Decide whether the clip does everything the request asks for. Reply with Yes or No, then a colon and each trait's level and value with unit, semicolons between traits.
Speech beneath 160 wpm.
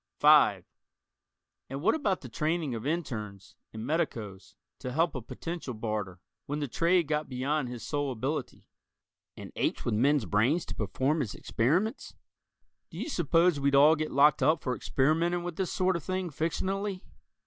No: average, 165 wpm